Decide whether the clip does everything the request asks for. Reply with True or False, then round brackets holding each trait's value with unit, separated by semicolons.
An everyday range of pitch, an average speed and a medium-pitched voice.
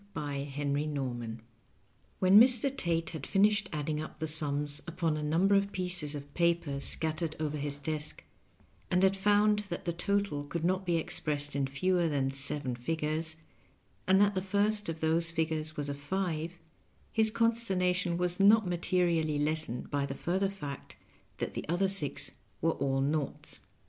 True (4.3 semitones; 165 wpm; 160 Hz)